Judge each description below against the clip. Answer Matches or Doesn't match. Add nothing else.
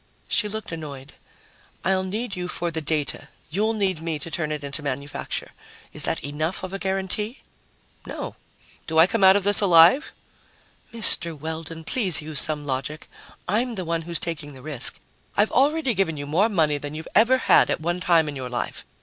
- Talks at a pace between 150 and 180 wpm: Doesn't match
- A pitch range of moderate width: Matches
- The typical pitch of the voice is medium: Matches